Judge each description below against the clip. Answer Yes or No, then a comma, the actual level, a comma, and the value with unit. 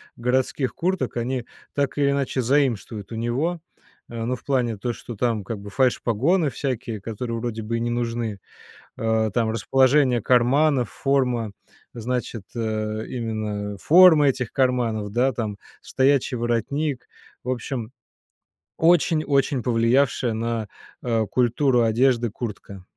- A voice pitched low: Yes, low, 120 Hz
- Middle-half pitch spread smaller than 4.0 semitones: Yes, average, 2.9 semitones